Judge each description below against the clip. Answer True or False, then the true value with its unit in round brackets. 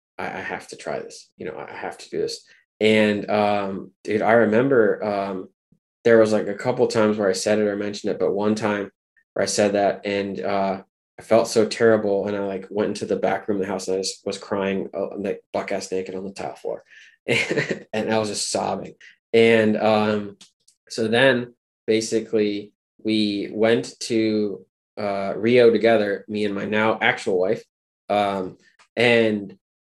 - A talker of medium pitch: False (105 Hz)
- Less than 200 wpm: True (185 wpm)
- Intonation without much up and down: True (1.9 semitones)